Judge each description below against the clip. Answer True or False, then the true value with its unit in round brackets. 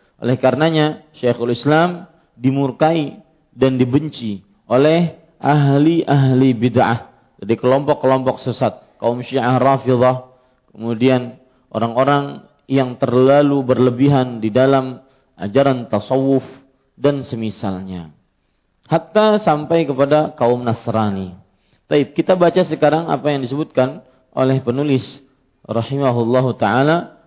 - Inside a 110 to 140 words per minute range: False (95 wpm)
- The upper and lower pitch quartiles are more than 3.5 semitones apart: False (2.7 semitones)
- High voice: False (130 Hz)